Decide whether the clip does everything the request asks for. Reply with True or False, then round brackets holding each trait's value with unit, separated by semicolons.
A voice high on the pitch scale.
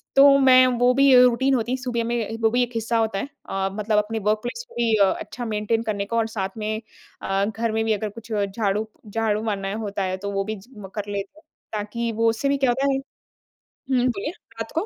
True (225 Hz)